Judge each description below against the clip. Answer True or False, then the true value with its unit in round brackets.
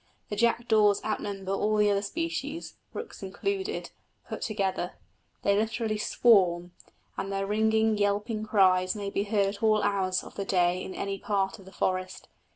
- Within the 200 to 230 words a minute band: False (160 wpm)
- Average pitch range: False (2.1 semitones)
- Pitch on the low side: False (205 Hz)